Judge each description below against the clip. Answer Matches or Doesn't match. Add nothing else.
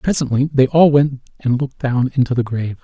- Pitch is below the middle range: Matches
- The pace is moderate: Doesn't match